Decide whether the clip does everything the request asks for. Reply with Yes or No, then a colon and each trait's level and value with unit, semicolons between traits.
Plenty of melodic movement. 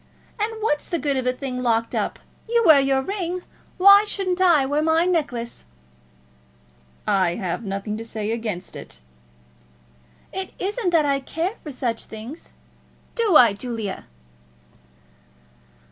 Yes: wide, 7.8 semitones